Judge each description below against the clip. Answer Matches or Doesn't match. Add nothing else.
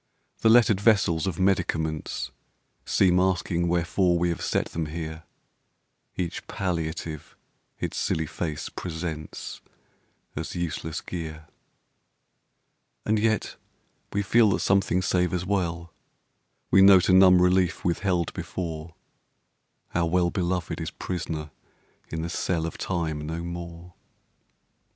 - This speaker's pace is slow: Matches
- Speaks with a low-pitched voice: Matches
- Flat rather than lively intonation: Matches